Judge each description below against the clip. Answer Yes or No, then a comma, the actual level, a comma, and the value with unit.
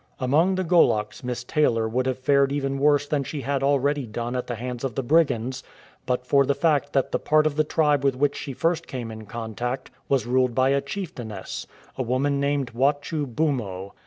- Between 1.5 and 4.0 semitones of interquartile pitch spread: Yes, average, 2.8 semitones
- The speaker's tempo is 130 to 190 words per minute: No, fast, 205 wpm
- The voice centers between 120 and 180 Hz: Yes, low, 135 Hz